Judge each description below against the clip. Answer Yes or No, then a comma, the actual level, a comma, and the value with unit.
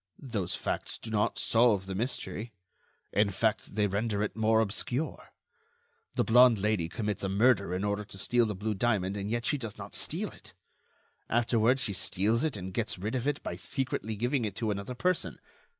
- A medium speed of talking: Yes, average, 190 wpm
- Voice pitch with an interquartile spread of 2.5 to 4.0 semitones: Yes, average, 3.1 semitones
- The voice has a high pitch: No, low, 110 Hz